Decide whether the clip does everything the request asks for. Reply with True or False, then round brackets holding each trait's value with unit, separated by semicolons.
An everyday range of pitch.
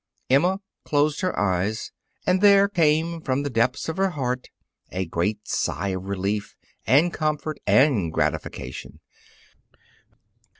False (8.1 semitones)